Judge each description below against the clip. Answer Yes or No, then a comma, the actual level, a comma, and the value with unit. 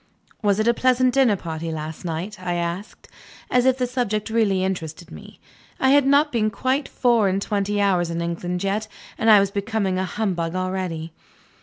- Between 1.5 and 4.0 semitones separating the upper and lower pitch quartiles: No, average, 4.6 semitones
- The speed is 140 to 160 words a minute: No, average, 185 wpm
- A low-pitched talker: No, high, 200 Hz